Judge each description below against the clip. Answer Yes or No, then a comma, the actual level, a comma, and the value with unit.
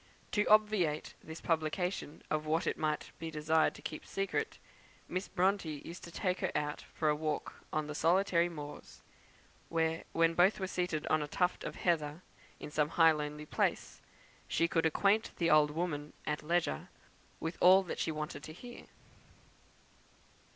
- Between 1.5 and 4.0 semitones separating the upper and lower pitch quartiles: Yes, average, 2.8 semitones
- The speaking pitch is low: No, medium, 160 Hz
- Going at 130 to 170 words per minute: Yes, average, 165 wpm